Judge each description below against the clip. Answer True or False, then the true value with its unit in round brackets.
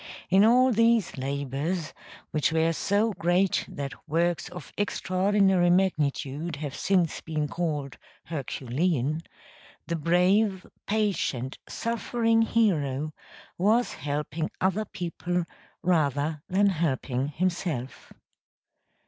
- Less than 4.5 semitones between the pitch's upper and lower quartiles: False (4.8 semitones)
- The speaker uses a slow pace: True (100 wpm)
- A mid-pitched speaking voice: True (170 Hz)